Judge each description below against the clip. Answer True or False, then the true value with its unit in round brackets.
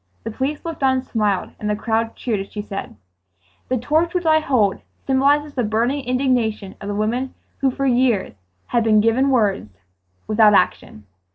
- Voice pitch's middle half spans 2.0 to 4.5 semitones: True (4.1 semitones)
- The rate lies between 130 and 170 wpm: False (180 wpm)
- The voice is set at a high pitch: True (240 Hz)